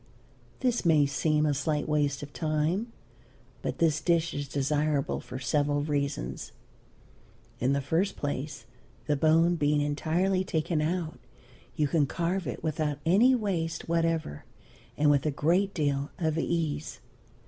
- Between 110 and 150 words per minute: Yes, average, 140 wpm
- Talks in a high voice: No, medium, 155 Hz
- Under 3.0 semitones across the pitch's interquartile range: Yes, narrow, 2.6 semitones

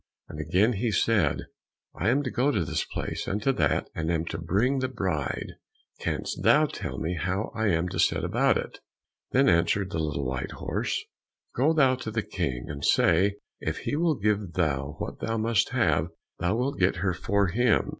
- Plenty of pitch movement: Yes, wide, 5.8 semitones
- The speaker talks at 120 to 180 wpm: No, average, 195 wpm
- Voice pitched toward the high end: No, very low, 95 Hz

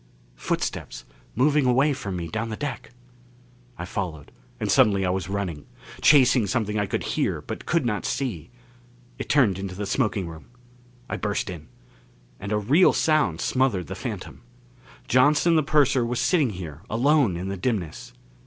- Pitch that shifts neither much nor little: No, wide, 6.5 semitones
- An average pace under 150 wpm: No, average, 160 wpm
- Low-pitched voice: Yes, low, 105 Hz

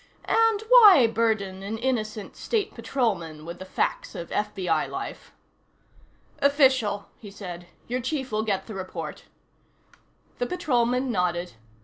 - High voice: Yes, high, 220 Hz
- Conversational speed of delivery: No, slow, 125 wpm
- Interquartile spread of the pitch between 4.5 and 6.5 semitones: Yes, wide, 5.6 semitones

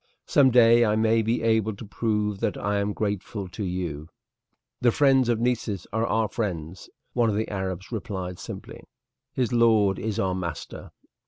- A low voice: Yes, low, 105 Hz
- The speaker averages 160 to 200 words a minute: Yes, average, 170 wpm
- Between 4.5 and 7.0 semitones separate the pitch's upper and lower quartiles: No, average, 3.1 semitones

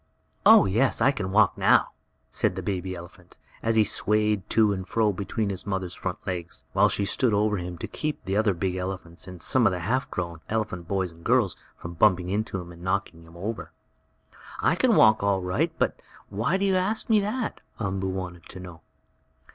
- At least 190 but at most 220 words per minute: Yes, fast, 205 wpm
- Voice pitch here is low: Yes, very low, 95 Hz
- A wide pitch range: No, average, 3.2 semitones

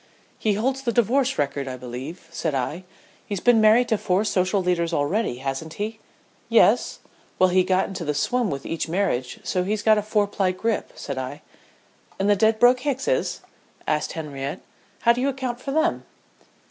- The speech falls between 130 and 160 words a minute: No, average, 185 wpm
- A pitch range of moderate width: No, wide, 6.6 semitones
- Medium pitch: No, high, 195 Hz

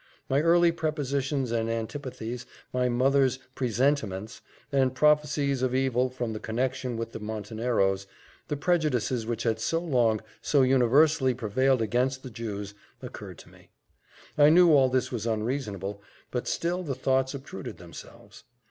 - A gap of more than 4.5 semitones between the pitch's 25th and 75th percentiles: No, average, 3.6 semitones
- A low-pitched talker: Yes, low, 130 Hz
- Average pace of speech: Yes, average, 145 wpm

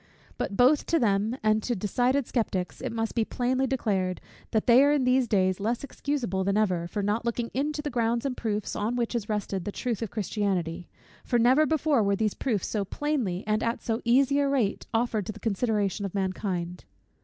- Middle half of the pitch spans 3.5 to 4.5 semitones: Yes, average, 4.0 semitones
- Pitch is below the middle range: No, high, 225 Hz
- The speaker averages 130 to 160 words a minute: No, fast, 205 wpm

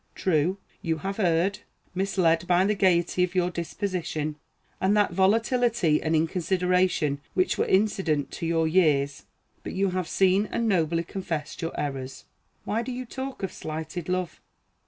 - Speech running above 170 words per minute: No, average, 155 wpm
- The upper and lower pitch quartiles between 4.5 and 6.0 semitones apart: No, average, 3.3 semitones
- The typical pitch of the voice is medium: Yes, medium, 180 Hz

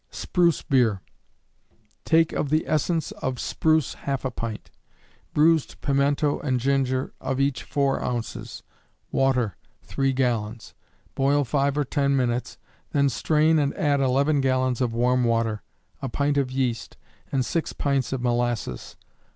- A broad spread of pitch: No, narrow, 2.6 semitones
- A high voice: No, low, 135 Hz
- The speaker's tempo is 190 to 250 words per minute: No, average, 140 wpm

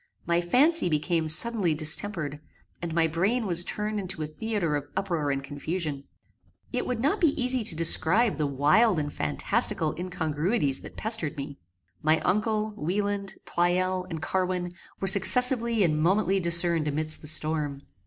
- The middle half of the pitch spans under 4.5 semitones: No, average, 5.2 semitones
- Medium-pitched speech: Yes, medium, 175 Hz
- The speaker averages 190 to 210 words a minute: No, average, 155 wpm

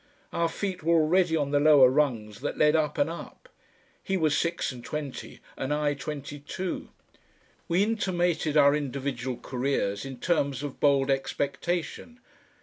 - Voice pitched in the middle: Yes, medium, 145 Hz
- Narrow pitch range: No, average, 3.5 semitones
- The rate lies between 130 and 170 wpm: Yes, average, 150 wpm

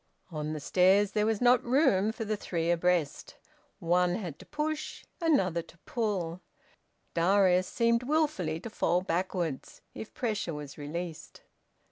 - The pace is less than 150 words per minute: Yes, average, 140 wpm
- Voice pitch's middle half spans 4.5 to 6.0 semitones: Yes, average, 4.9 semitones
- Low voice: No, medium, 185 Hz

